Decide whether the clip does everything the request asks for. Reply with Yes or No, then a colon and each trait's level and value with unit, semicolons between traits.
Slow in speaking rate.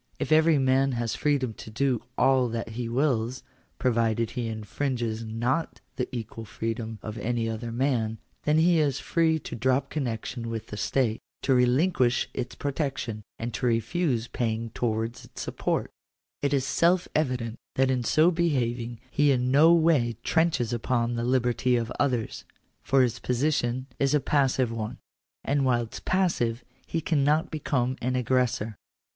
No: average, 160 wpm